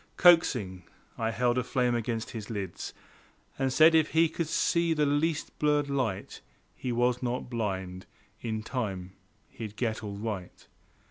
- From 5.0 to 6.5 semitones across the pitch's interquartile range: Yes, wide, 5.4 semitones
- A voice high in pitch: No, low, 120 Hz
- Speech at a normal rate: Yes, average, 150 wpm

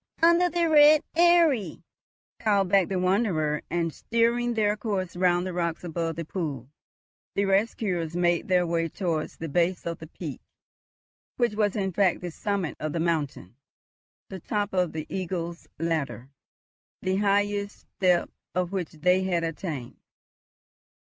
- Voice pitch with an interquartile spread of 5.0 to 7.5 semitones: No, average, 3.6 semitones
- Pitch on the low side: No, medium, 180 Hz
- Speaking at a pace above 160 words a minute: No, average, 145 wpm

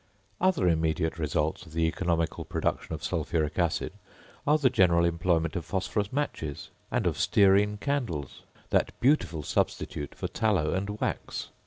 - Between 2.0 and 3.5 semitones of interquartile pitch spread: No, average, 4.3 semitones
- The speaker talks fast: No, average, 145 wpm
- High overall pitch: No, very low, 85 Hz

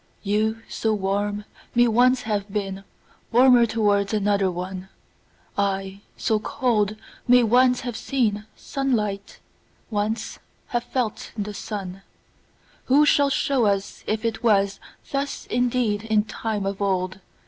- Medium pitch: No, high, 215 Hz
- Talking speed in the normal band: No, slow, 110 wpm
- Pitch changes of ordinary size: Yes, average, 3.2 semitones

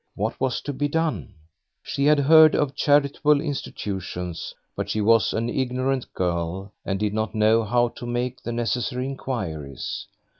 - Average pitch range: Yes, average, 5.0 semitones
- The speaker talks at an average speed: Yes, average, 155 wpm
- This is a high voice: No, low, 120 Hz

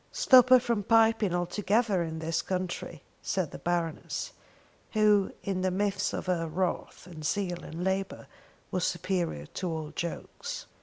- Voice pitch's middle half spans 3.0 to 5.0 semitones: Yes, average, 3.3 semitones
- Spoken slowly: No, average, 150 wpm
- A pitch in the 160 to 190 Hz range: Yes, medium, 185 Hz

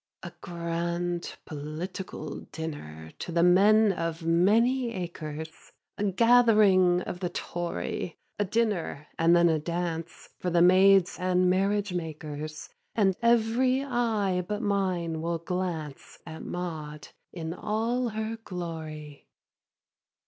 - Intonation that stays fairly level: No, average, 4.0 semitones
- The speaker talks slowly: Yes, slow, 120 wpm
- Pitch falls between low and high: Yes, medium, 180 Hz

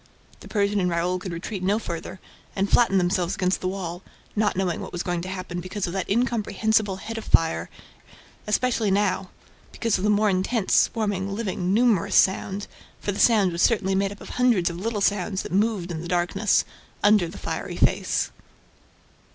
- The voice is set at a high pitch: Yes, high, 195 Hz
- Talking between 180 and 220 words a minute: Yes, average, 190 wpm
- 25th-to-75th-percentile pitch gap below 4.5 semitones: Yes, narrow, 2.6 semitones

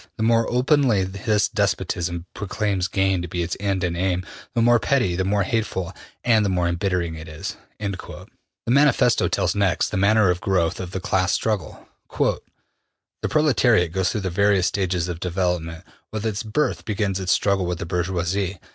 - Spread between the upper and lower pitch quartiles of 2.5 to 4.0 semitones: Yes, average, 3.1 semitones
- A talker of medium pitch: No, very low, 95 Hz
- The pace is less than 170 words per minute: No, average, 175 wpm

